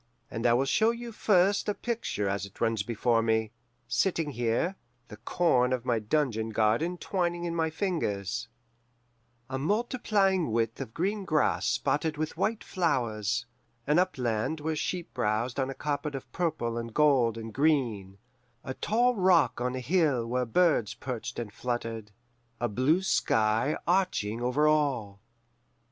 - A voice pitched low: Yes, low, 130 Hz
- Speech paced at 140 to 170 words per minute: Yes, average, 155 wpm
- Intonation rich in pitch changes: Yes, wide, 7.0 semitones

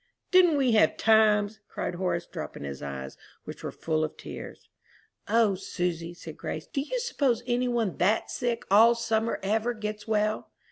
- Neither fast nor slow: Yes, average, 170 wpm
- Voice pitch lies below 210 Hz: No, high, 215 Hz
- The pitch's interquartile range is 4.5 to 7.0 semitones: Yes, average, 4.8 semitones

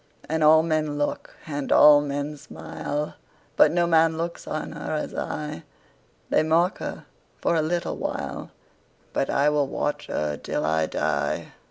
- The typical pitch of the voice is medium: Yes, medium, 150 Hz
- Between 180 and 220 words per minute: No, average, 145 wpm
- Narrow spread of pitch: Yes, narrow, 1.9 semitones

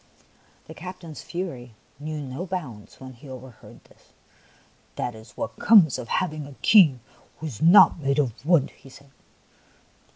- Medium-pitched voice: Yes, medium, 145 Hz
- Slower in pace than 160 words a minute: No, average, 165 wpm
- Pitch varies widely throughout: No, average, 4.9 semitones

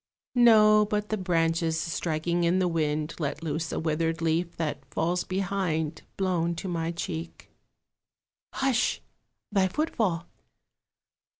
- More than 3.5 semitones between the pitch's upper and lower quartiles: No, average, 2.8 semitones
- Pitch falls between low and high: Yes, medium, 170 Hz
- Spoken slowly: Yes, slow, 120 wpm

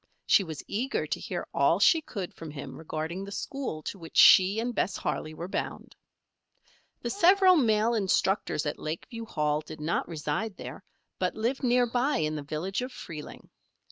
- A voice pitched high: Yes, high, 195 Hz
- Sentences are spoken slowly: No, average, 175 wpm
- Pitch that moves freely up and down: Yes, wide, 7.5 semitones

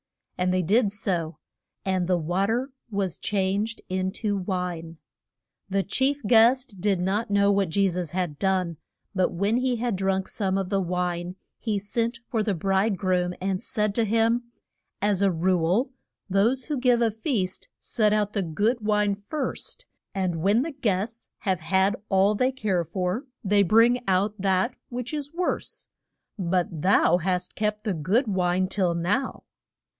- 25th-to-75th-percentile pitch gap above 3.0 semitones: Yes, average, 3.6 semitones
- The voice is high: Yes, high, 195 Hz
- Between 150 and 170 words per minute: Yes, average, 165 wpm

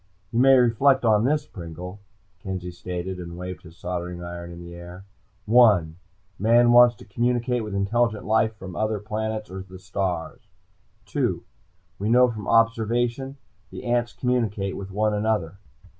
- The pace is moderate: Yes, average, 155 wpm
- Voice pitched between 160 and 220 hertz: No, low, 105 Hz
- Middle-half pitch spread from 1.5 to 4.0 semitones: No, average, 4.6 semitones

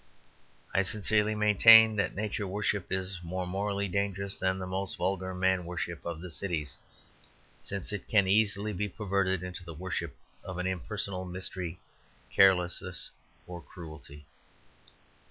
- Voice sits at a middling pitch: No, very low, 95 Hz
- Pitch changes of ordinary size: No, narrow, 2.0 semitones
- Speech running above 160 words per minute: No, slow, 135 wpm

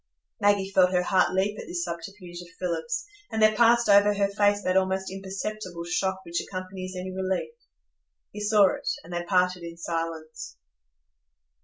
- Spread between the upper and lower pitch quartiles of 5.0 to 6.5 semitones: No, narrow, 2.5 semitones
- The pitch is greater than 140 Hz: Yes, high, 190 Hz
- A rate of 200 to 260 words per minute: No, average, 165 wpm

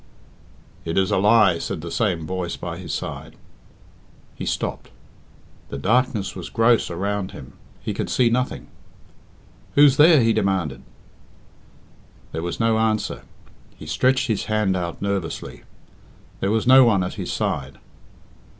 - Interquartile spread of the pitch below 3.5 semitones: No, average, 4.7 semitones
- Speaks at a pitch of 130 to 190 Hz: No, low, 100 Hz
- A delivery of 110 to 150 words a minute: Yes, average, 140 wpm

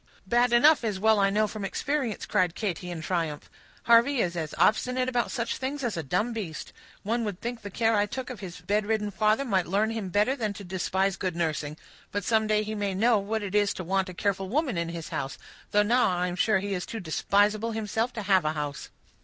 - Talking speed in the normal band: No, fast, 230 wpm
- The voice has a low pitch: No, high, 205 Hz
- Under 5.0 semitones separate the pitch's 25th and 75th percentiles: Yes, average, 3.5 semitones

